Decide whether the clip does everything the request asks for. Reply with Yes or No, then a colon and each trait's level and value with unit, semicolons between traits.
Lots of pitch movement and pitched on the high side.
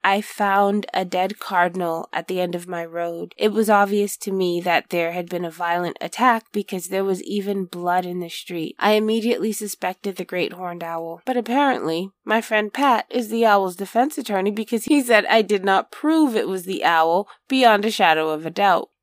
No: average, 3.5 semitones; high, 195 Hz